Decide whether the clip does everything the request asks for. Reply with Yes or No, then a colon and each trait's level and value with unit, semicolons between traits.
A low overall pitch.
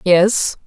No: high, 190 Hz